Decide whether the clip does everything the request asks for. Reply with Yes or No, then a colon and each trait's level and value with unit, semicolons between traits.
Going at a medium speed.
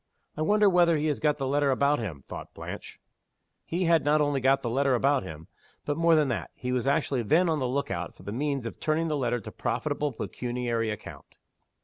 No: fast, 225 wpm